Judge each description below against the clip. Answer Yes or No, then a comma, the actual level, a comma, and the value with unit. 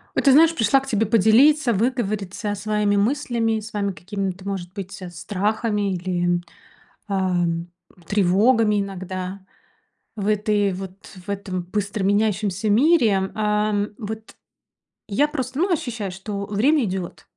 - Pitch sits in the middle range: No, high, 205 Hz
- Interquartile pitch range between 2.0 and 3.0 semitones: Yes, narrow, 2.6 semitones